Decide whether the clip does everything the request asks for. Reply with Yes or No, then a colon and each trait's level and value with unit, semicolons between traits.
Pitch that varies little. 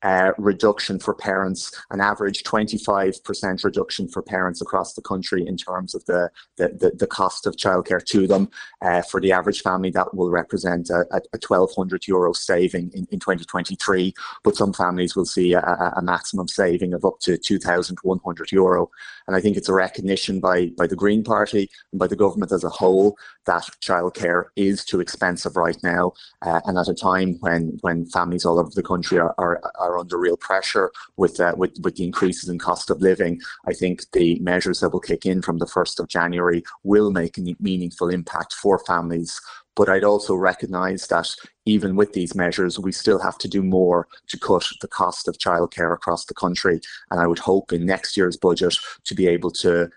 Yes: narrow, 1.8 semitones